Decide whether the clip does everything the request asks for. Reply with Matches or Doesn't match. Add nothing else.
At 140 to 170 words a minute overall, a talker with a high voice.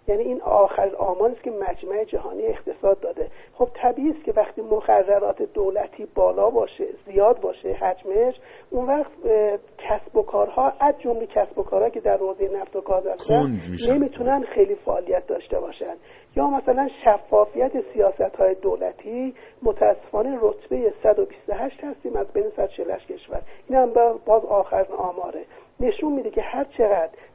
Matches